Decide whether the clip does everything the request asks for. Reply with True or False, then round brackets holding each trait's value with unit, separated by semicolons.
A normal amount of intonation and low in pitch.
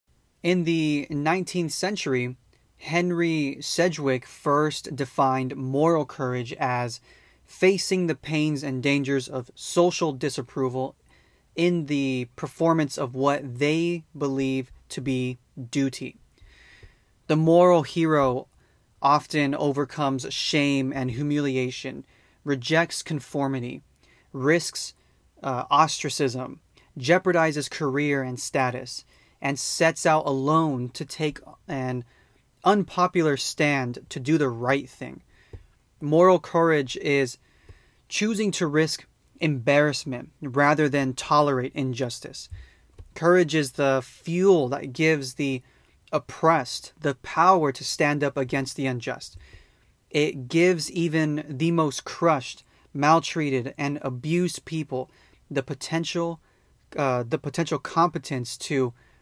False (3.5 semitones; 145 Hz)